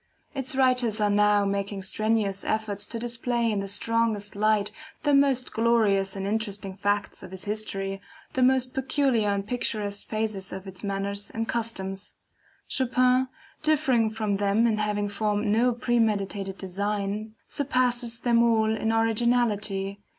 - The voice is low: No, high, 215 Hz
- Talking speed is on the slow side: No, average, 145 wpm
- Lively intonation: No, average, 2.8 semitones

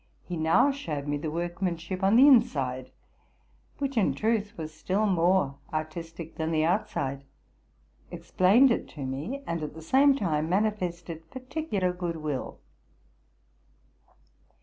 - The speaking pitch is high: No, medium, 175 Hz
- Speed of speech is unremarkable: No, slow, 130 wpm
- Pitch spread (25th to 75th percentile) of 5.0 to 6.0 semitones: Yes, wide, 5.4 semitones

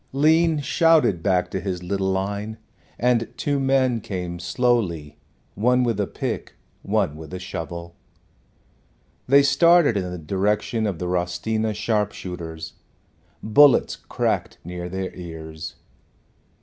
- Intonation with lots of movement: Yes, wide, 5.8 semitones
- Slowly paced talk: Yes, slow, 125 wpm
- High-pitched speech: No, low, 100 Hz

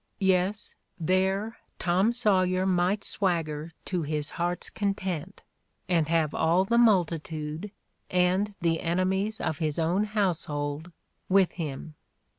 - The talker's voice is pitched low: No, medium, 180 Hz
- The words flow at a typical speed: No, slow, 115 wpm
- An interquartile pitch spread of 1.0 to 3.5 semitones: Yes, average, 3.2 semitones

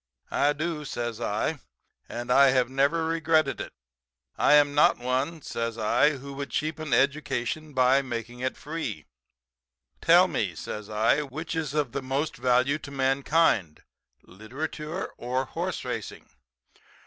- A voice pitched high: No, medium, 140 Hz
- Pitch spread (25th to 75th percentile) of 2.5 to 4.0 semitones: Yes, average, 3.7 semitones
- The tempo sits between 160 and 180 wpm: No, average, 140 wpm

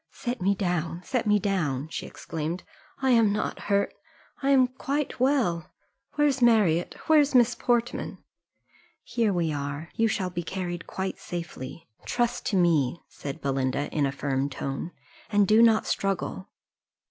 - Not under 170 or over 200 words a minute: No, average, 150 wpm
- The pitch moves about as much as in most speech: No, wide, 6.6 semitones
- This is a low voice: No, high, 190 Hz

